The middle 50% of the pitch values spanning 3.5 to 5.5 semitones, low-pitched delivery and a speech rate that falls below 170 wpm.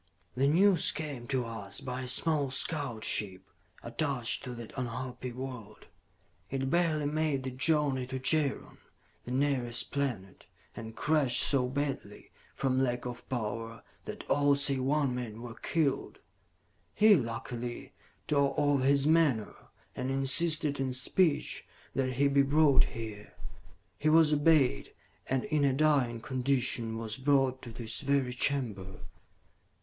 No: average, 3.0 semitones; low, 130 Hz; average, 140 wpm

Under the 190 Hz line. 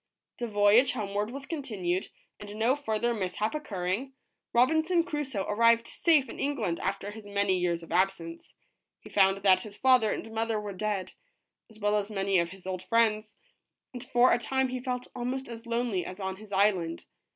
No: high, 215 Hz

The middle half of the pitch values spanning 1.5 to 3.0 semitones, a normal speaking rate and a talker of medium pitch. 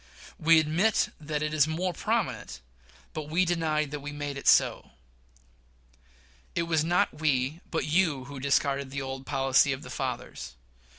Yes: average, 2.7 semitones; average, 160 wpm; medium, 150 Hz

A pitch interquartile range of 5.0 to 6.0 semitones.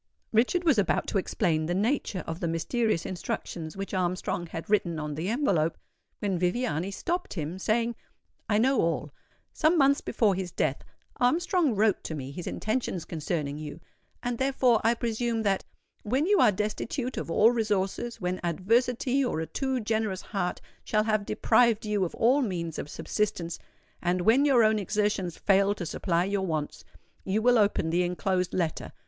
Yes: average, 5.3 semitones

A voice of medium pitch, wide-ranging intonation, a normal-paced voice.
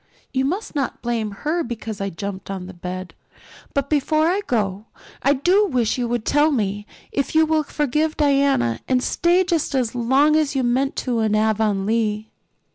No: very high, 250 Hz; wide, 5.8 semitones; average, 180 wpm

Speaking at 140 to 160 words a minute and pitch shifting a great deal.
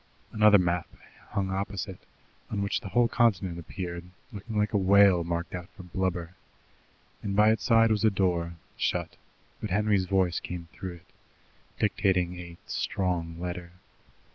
No: average, 150 wpm; average, 2.8 semitones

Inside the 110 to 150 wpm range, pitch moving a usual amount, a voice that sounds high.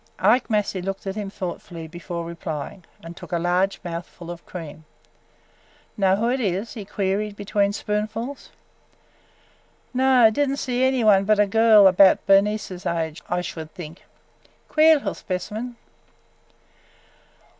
Yes: average, 140 wpm; average, 3.7 semitones; high, 195 Hz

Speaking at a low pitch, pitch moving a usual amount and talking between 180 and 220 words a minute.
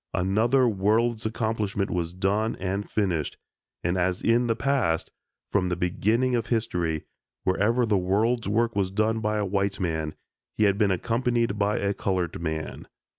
No: low, 100 Hz; average, 3.7 semitones; average, 160 wpm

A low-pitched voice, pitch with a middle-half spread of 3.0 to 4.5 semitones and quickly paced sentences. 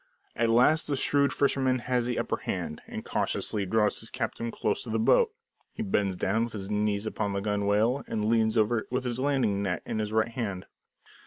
Yes: low, 110 Hz; average, 3.3 semitones; fast, 210 wpm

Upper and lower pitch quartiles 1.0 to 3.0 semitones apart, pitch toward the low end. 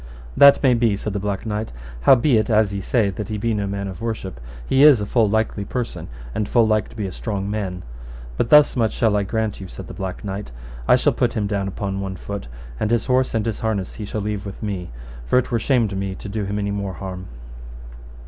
Yes: narrow, 2.4 semitones; low, 105 Hz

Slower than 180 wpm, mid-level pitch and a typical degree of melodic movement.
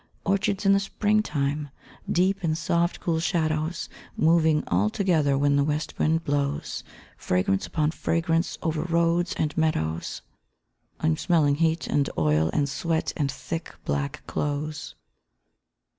Yes: average, 140 wpm; medium, 155 Hz; average, 3.0 semitones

